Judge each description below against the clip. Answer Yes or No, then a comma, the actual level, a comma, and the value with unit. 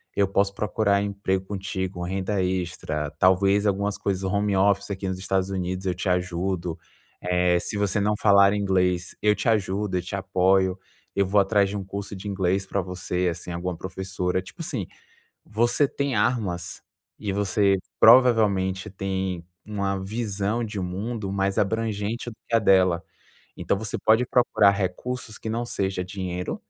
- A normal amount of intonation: No, narrow, 1.8 semitones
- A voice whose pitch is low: Yes, very low, 95 Hz